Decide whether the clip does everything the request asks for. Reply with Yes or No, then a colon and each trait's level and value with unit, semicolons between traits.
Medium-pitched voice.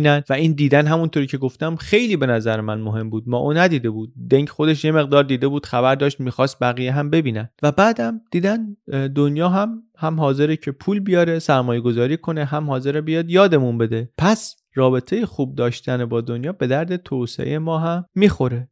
Yes: medium, 145 Hz